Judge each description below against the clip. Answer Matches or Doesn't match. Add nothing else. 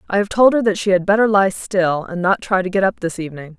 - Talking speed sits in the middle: Doesn't match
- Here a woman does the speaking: Matches